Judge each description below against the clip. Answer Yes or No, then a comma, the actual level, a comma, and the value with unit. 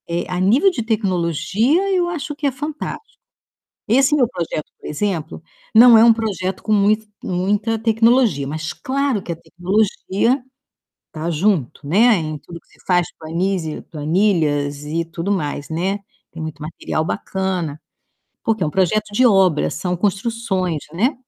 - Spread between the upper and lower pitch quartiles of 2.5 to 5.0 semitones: No, wide, 5.5 semitones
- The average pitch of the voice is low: No, high, 190 Hz